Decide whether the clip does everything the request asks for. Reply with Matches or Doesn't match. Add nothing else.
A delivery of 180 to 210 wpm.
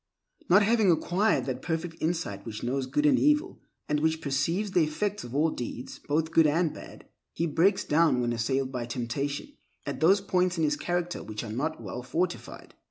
Matches